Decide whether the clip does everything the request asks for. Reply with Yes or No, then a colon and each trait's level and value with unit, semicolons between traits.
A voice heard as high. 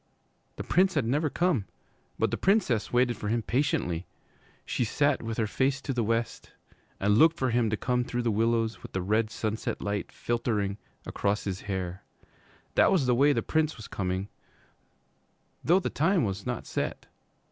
No: low, 115 Hz